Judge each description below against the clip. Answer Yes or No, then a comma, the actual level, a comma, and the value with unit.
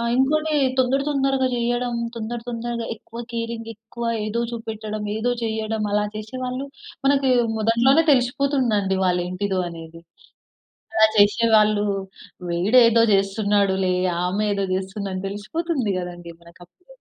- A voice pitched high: Yes, high, 220 Hz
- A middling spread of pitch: Yes, average, 3.6 semitones